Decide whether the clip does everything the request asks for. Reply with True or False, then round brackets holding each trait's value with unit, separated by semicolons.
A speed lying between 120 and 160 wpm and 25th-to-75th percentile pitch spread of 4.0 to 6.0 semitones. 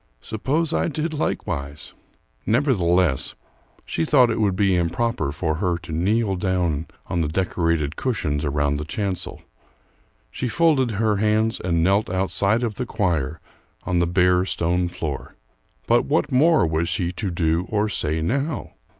True (150 wpm; 5.1 semitones)